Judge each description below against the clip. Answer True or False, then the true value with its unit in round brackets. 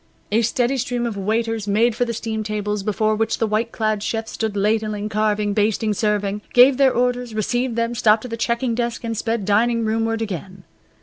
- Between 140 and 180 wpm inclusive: False (195 wpm)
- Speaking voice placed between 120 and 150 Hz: False (220 Hz)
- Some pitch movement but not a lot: False (1.9 semitones)